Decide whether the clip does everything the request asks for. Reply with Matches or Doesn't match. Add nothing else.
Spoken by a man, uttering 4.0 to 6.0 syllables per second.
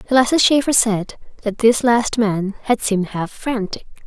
Doesn't match